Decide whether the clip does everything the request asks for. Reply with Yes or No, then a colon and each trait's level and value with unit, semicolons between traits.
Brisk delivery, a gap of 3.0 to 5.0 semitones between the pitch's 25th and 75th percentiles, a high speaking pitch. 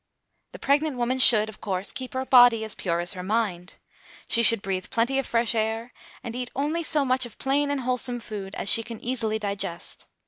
Yes: fast, 210 wpm; average, 3.5 semitones; high, 230 Hz